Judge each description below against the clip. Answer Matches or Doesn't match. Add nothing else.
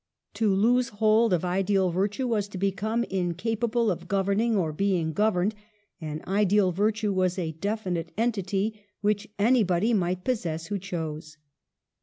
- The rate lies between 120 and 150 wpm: Matches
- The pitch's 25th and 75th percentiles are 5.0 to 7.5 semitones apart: Doesn't match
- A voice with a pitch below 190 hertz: Doesn't match